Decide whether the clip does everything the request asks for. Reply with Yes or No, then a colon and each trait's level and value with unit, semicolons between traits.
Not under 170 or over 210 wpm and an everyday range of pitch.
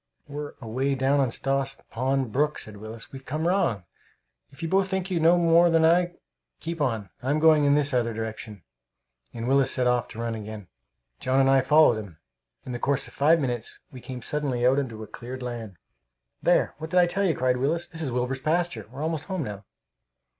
Yes: fast, 205 wpm; average, 4.8 semitones